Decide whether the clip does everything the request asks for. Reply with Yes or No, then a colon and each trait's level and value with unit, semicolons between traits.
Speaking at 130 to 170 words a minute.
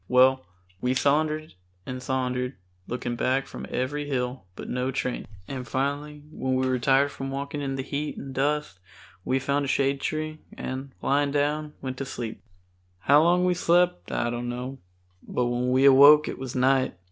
No: average, 180 wpm